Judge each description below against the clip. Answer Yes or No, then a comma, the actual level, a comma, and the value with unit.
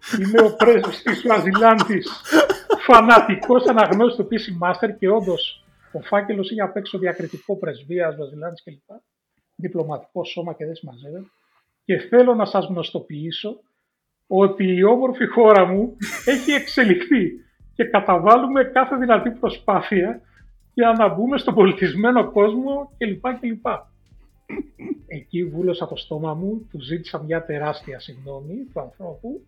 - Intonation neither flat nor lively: Yes, average, 4.8 semitones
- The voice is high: Yes, high, 205 Hz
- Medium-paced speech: Yes, average, 125 wpm